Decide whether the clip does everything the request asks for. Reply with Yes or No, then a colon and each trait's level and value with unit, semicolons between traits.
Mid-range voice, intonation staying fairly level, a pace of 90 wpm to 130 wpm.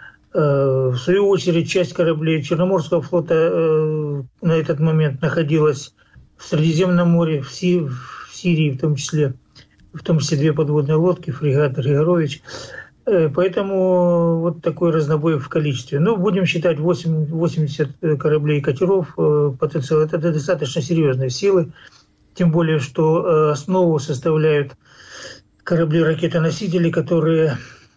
Yes: medium, 160 Hz; narrow, 2.3 semitones; average, 115 wpm